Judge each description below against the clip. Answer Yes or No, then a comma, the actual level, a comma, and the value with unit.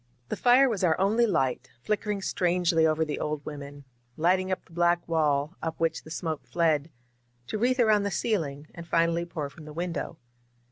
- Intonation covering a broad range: No, average, 3.5 semitones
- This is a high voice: No, medium, 170 Hz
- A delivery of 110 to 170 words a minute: No, average, 185 wpm